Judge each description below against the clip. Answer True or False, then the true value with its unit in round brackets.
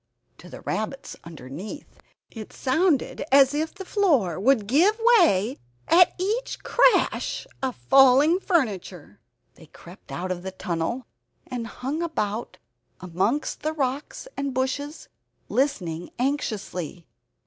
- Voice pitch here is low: False (255 Hz)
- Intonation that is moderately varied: False (8.1 semitones)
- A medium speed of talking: False (120 wpm)